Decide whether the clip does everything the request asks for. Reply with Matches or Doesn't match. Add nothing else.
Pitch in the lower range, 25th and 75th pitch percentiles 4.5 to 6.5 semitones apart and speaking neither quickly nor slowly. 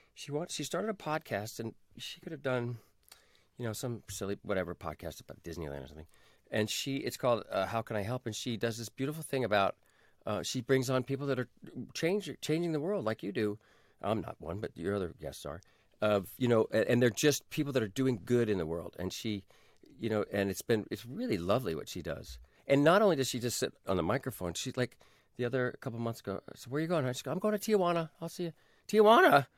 Doesn't match